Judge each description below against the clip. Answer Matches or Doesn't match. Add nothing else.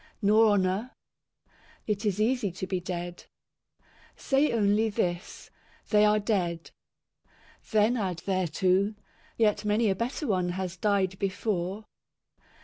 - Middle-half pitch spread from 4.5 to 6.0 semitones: Doesn't match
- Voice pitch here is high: Matches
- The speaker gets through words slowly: Matches